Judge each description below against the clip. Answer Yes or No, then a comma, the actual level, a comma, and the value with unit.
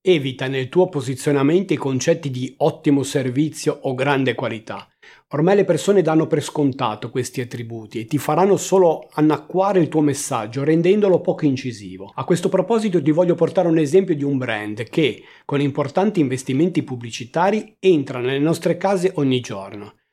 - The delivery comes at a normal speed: Yes, average, 160 wpm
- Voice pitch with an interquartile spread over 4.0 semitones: Yes, average, 5.1 semitones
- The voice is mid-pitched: Yes, medium, 145 Hz